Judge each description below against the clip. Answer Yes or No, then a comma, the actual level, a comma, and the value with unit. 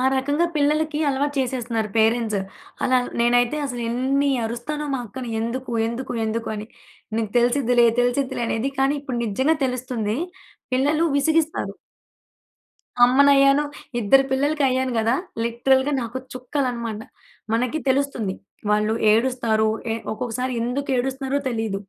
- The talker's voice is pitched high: Yes, very high, 255 Hz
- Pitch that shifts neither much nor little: Yes, average, 3.1 semitones